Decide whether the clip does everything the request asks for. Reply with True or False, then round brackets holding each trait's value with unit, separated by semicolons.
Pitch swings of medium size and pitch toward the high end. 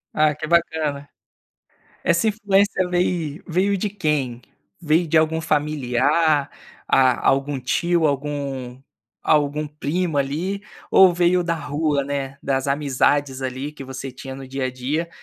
False (3.7 semitones; 150 Hz)